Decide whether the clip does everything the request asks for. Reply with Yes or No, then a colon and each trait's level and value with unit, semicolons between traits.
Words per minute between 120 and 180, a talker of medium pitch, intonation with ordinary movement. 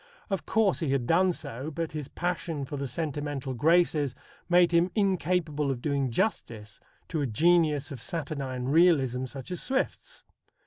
Yes: average, 155 wpm; medium, 150 Hz; average, 4.4 semitones